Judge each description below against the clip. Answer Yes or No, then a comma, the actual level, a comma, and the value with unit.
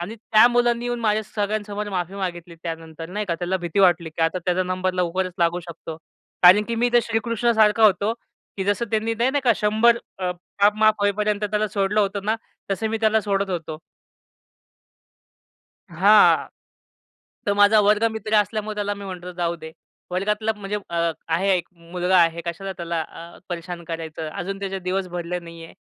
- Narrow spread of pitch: No, average, 3.5 semitones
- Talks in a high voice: Yes, high, 195 Hz